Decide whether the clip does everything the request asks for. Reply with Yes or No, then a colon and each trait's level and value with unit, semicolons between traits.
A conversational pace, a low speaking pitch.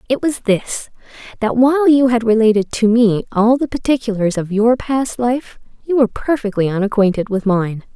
No: average, 165 wpm; high, 235 Hz